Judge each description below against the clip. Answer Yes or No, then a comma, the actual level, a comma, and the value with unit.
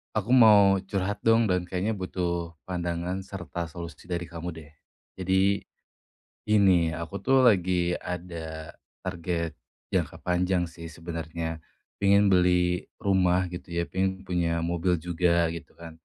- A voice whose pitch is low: Yes, very low, 90 Hz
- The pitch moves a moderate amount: No, narrow, 2.1 semitones